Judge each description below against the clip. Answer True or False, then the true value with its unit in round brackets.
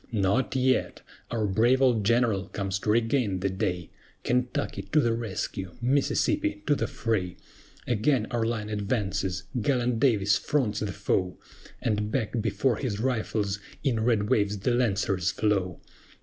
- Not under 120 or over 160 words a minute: True (145 wpm)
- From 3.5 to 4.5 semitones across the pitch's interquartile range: True (3.9 semitones)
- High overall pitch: False (110 Hz)